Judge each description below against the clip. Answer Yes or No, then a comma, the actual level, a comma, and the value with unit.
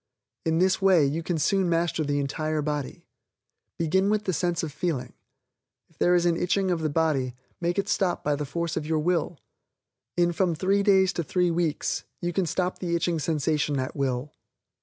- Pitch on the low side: No, medium, 165 Hz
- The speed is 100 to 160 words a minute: No, average, 195 wpm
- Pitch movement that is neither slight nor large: Yes, average, 3.0 semitones